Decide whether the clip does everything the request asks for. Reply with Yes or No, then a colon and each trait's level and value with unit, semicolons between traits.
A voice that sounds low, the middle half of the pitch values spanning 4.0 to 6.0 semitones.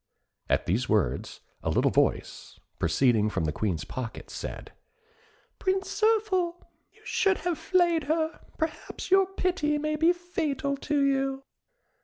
No: very high, 310 Hz; average, 5.1 semitones